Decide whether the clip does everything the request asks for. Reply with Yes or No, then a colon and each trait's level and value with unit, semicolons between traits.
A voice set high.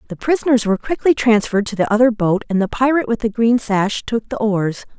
Yes: high, 225 Hz